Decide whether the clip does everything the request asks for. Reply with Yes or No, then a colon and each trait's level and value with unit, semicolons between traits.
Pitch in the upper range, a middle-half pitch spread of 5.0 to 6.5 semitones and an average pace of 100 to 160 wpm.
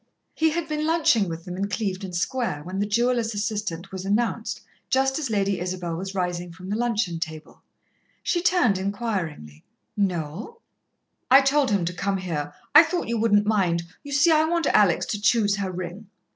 No: high, 205 Hz; wide, 5.4 semitones; average, 180 wpm